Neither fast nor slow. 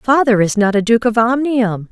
No: fast, 220 wpm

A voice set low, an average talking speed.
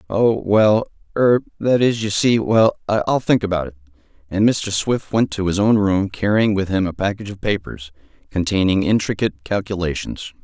Yes: low, 100 Hz; average, 160 wpm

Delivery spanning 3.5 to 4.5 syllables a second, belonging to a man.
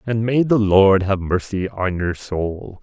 Yes: 3.7 syllables/s; male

